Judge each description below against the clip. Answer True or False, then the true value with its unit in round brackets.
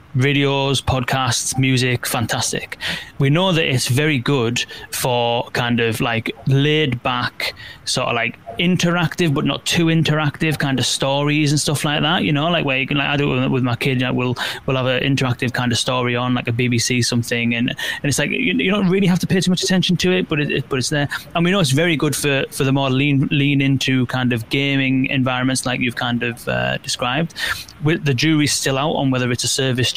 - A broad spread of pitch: False (3.2 semitones)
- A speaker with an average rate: False (225 wpm)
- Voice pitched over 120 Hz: True (135 Hz)